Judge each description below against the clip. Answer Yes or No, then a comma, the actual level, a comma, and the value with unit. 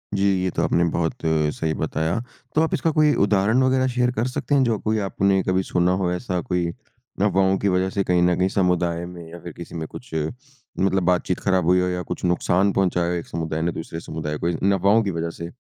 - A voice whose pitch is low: Yes, very low, 90 Hz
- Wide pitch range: No, average, 2.9 semitones